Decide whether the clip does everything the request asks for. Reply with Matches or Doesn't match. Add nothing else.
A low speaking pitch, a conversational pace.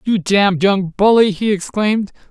Doesn't match